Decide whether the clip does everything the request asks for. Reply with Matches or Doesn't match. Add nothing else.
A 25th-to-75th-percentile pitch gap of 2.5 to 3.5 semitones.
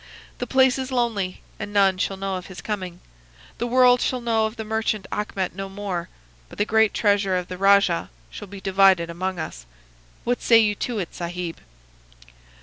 Matches